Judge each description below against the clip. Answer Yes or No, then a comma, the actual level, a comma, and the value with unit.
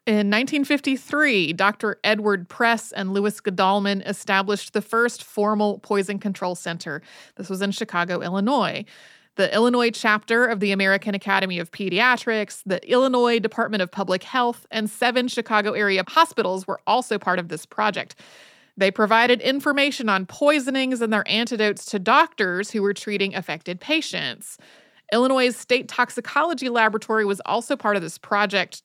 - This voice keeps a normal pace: Yes, average, 150 wpm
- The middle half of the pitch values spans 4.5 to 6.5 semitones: No, average, 3.6 semitones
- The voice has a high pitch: Yes, high, 210 Hz